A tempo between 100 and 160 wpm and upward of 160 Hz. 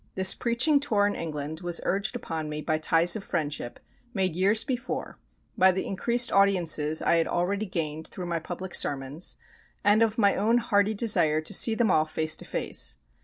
No: average, 185 wpm; medium, 185 Hz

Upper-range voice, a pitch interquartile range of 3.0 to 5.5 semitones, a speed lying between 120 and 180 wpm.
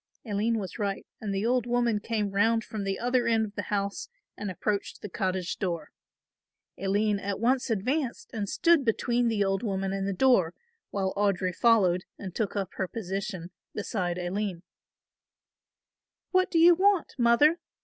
Yes: high, 205 Hz; average, 3.4 semitones; average, 165 wpm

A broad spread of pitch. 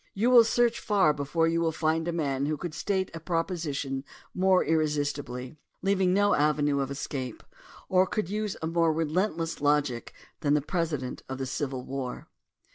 No: average, 4.2 semitones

